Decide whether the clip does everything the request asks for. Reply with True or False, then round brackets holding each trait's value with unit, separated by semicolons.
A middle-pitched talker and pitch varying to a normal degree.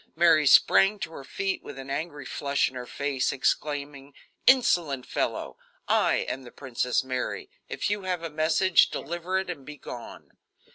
True (150 Hz; 4.4 semitones)